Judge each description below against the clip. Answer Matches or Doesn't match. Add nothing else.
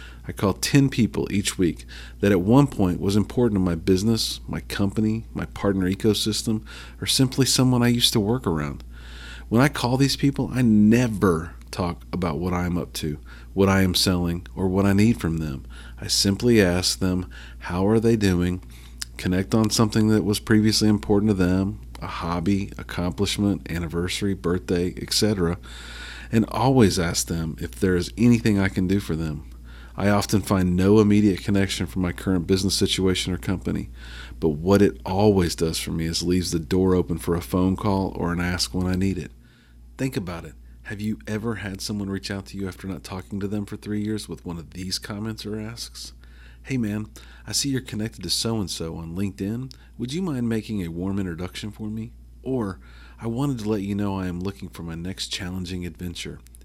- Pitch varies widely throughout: Doesn't match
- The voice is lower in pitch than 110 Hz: Matches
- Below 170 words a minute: Doesn't match